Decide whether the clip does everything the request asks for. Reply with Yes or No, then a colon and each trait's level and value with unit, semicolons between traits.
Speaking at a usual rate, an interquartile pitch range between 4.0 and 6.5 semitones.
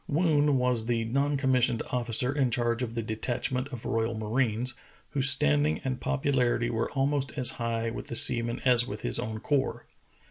No: average, 175 wpm; narrow, 2.6 semitones